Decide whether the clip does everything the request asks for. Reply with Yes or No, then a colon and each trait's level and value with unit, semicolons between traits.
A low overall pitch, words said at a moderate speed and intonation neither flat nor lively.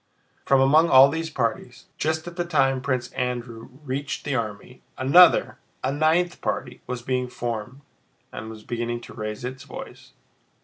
Yes: low, 130 Hz; average, 160 wpm; average, 3.6 semitones